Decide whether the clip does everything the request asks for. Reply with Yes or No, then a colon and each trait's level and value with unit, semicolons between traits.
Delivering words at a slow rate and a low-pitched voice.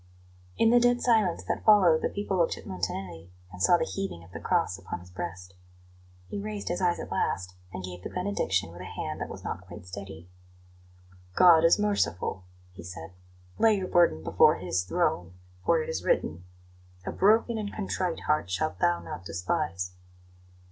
No: average, 180 wpm; low, 100 Hz